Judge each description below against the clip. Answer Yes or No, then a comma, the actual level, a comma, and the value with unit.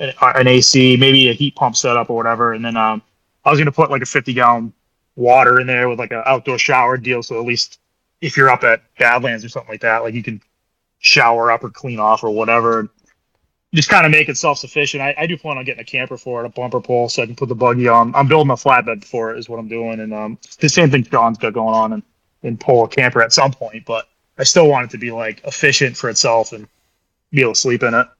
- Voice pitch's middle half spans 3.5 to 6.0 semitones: No, average, 2.7 semitones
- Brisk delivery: Yes, fast, 260 wpm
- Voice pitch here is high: No, low, 120 Hz